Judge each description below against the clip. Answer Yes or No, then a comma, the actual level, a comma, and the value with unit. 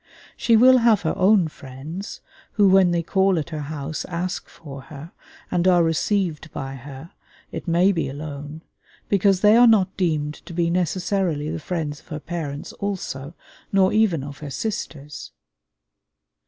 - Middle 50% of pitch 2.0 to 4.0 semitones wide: No, average, 4.4 semitones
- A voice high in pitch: No, medium, 170 Hz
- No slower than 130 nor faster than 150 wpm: No, average, 160 wpm